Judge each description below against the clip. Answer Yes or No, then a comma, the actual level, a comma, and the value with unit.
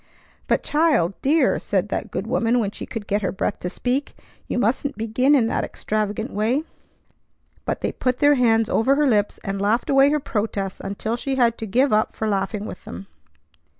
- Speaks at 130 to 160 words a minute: No, average, 195 wpm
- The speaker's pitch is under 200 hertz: No, high, 225 Hz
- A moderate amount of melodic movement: Yes, average, 4.3 semitones